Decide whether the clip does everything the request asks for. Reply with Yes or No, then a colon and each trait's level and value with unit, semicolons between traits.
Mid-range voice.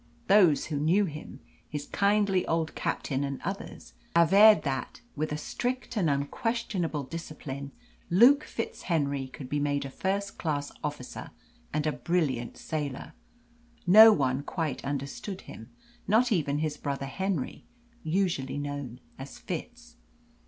Yes: medium, 155 Hz